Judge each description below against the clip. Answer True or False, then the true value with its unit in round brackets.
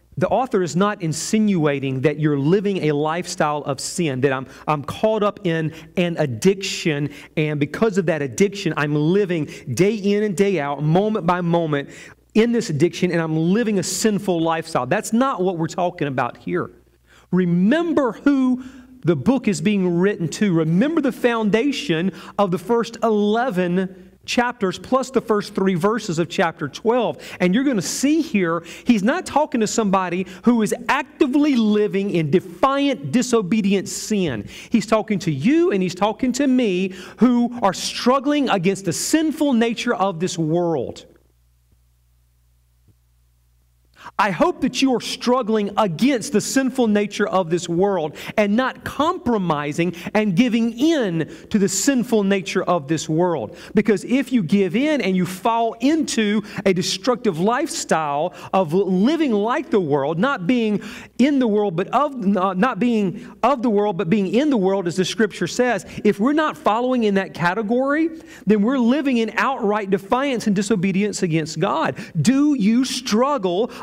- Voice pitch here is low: False (200 Hz)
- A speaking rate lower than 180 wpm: True (160 wpm)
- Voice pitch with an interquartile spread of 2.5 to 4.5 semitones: False (5.3 semitones)